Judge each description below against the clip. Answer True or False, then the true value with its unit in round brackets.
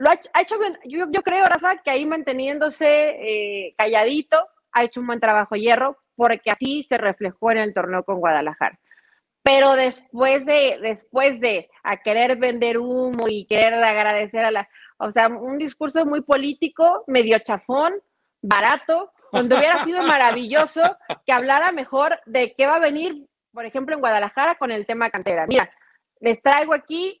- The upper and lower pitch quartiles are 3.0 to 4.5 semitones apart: False (5.3 semitones)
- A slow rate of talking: False (165 wpm)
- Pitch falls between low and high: False (265 Hz)